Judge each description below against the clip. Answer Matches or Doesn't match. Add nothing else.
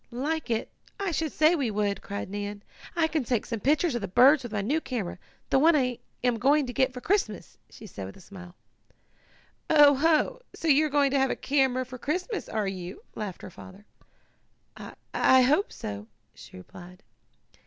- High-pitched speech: Matches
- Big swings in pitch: Matches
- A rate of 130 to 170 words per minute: Doesn't match